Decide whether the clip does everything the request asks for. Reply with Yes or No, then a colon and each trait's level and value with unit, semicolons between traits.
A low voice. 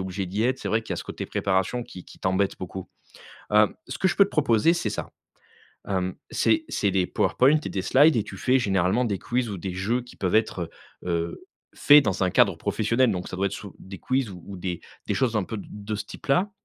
Yes: low, 105 Hz